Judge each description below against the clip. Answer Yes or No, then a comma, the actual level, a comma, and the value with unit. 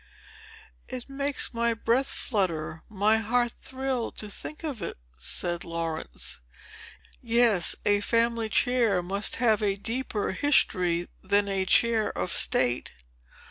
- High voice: Yes, high, 215 Hz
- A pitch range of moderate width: Yes, average, 4.3 semitones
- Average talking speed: No, slow, 115 wpm